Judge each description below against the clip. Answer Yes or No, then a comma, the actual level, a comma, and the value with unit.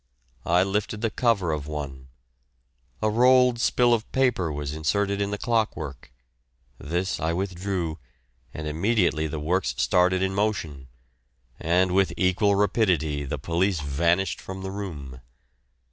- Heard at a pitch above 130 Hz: No, very low, 90 Hz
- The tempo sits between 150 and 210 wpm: No, average, 140 wpm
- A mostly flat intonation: No, average, 4.7 semitones